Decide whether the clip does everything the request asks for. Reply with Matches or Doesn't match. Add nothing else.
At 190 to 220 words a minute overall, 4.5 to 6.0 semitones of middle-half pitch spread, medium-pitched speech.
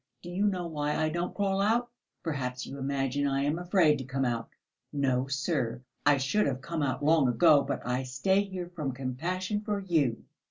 Matches